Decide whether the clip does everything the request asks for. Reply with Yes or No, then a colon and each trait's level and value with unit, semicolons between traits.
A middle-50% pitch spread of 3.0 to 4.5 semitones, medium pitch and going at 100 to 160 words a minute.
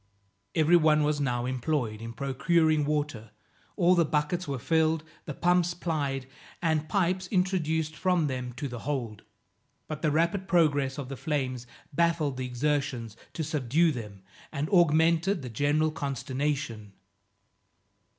Yes: average, 3.9 semitones; medium, 150 Hz; average, 140 wpm